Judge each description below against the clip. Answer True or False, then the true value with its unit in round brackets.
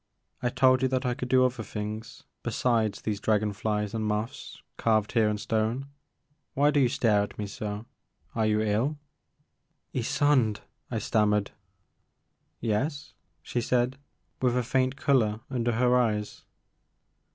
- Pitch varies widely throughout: False (3.3 semitones)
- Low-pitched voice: True (115 Hz)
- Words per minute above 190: False (150 wpm)